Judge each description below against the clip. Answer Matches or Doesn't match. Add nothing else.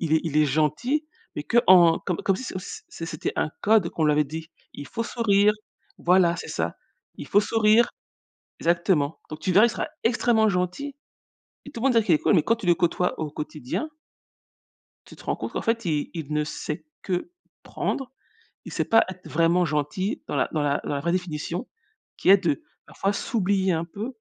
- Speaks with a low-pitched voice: Doesn't match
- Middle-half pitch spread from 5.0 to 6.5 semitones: Matches